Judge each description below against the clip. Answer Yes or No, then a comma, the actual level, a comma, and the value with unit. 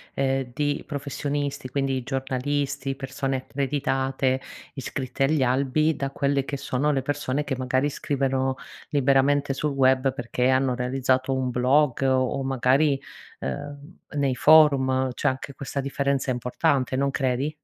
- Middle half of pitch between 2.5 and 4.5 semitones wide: No, narrow, 1.5 semitones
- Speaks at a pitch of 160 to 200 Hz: No, low, 135 Hz